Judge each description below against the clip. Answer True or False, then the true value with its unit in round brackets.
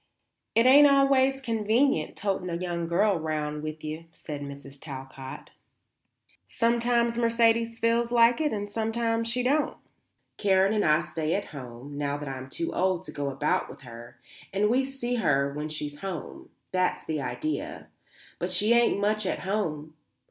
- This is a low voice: False (190 Hz)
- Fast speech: False (165 wpm)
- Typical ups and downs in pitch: False (7.5 semitones)